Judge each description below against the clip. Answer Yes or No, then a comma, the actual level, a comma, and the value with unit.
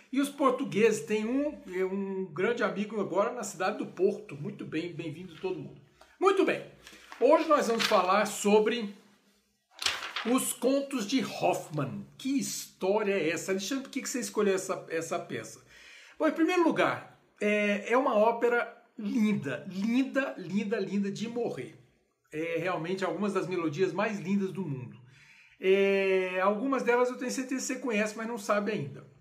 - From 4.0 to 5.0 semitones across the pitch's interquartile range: Yes, average, 4.4 semitones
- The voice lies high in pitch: Yes, high, 210 Hz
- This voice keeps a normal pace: Yes, average, 155 wpm